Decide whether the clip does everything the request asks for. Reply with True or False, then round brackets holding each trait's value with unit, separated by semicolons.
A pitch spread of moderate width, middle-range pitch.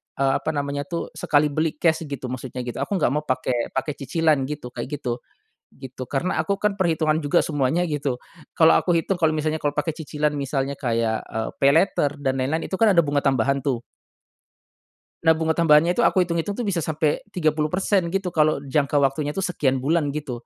True (3.1 semitones; 150 Hz)